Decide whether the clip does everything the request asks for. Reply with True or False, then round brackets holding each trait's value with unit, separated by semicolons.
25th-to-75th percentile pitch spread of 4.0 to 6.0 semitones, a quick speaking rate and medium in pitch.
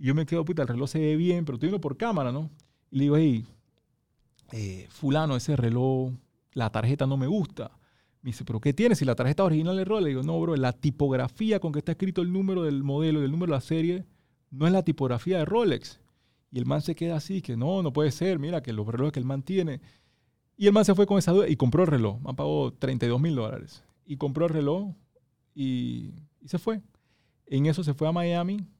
True (4.8 semitones; 240 wpm; 150 Hz)